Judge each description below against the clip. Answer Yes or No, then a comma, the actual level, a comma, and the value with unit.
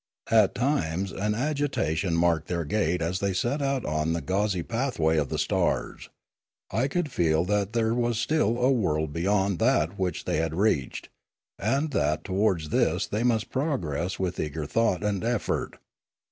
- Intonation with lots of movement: Yes, wide, 6.1 semitones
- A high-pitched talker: No, low, 100 Hz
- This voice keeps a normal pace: Yes, average, 165 wpm